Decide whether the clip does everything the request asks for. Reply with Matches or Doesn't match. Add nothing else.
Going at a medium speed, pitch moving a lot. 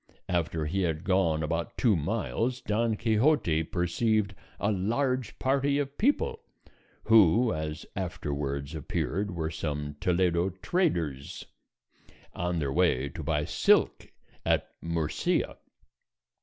Doesn't match